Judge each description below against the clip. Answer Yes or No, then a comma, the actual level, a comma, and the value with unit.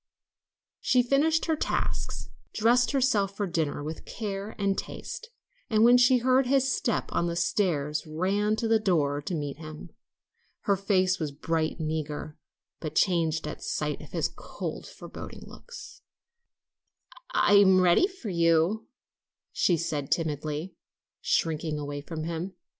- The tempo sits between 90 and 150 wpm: Yes, average, 145 wpm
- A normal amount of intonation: No, wide, 5.9 semitones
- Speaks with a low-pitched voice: No, medium, 180 Hz